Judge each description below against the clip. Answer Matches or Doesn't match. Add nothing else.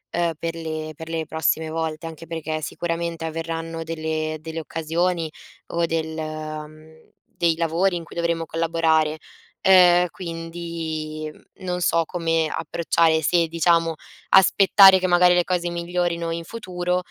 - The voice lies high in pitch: Doesn't match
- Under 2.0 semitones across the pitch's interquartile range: Matches